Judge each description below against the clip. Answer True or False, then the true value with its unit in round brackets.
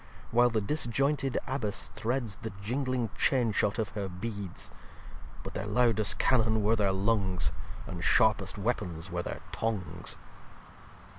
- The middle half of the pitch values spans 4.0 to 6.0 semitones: False (3.6 semitones)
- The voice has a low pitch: True (110 Hz)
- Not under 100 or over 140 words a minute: True (135 wpm)